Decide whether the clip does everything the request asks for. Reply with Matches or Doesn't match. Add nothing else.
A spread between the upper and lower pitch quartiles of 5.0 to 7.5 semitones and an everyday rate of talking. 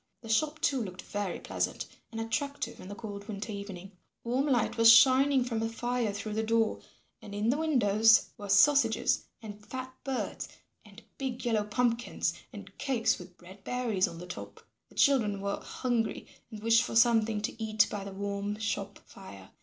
Doesn't match